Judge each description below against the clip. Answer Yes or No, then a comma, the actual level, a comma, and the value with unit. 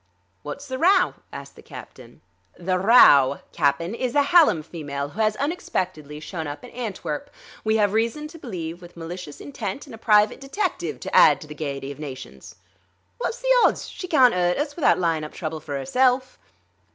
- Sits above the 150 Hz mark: Yes, medium, 185 Hz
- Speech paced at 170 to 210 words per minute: Yes, average, 185 wpm